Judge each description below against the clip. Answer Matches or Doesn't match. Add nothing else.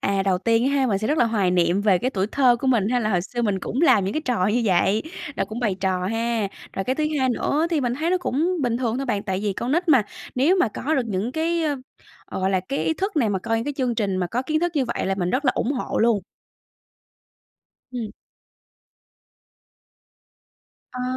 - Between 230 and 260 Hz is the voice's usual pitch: Matches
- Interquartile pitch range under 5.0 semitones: Doesn't match